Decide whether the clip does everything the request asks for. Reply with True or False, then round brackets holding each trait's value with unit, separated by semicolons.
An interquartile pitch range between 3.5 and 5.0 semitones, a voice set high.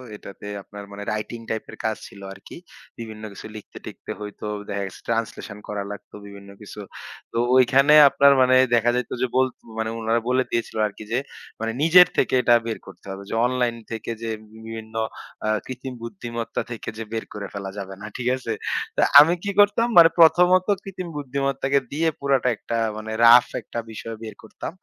False (3.8 semitones; 115 Hz)